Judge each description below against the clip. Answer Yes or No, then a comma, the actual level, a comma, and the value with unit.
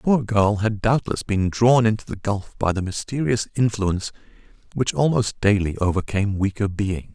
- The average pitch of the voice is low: Yes, low, 105 Hz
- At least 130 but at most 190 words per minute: Yes, average, 170 wpm